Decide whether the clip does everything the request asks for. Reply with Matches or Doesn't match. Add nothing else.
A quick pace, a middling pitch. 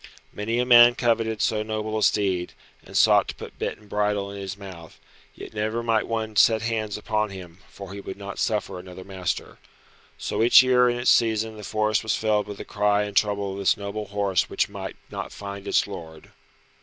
Doesn't match